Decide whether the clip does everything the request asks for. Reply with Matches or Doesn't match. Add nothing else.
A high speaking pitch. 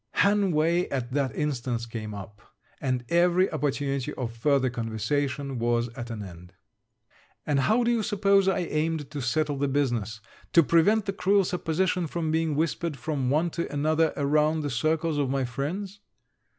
Doesn't match